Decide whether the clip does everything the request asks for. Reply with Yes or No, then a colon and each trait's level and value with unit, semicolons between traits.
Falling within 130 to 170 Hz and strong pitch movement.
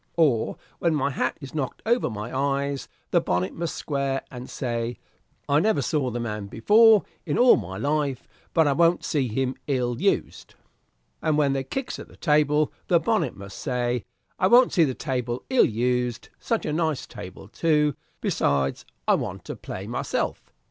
No: medium, 140 Hz; average, 4.4 semitones